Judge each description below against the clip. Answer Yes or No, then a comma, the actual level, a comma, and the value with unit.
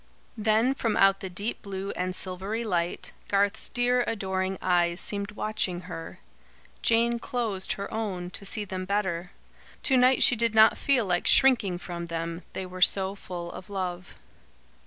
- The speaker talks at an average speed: Yes, average, 160 wpm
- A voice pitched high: Yes, high, 195 Hz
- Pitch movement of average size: Yes, average, 3.3 semitones